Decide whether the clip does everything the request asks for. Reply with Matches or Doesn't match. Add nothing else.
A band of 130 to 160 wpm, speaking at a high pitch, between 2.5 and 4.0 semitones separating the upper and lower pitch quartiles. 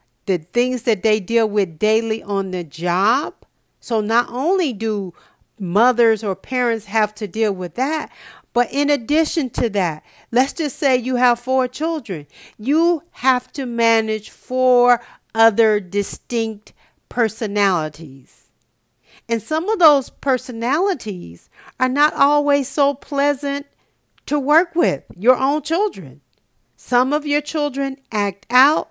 Doesn't match